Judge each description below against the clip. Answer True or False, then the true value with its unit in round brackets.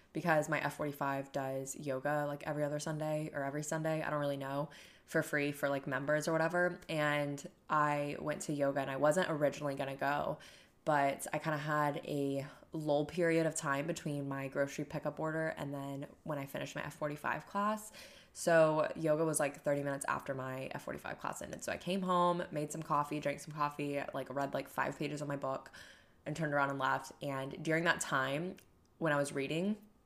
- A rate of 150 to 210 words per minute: True (200 wpm)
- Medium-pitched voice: True (150 Hz)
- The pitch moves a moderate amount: False (2.1 semitones)